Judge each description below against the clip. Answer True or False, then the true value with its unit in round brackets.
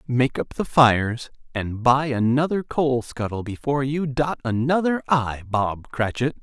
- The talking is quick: False (150 wpm)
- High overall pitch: False (130 Hz)